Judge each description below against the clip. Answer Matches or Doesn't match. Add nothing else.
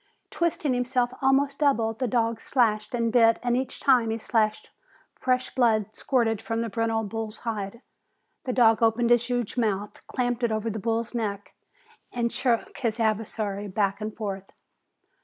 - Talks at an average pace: Matches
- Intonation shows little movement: Matches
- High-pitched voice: Matches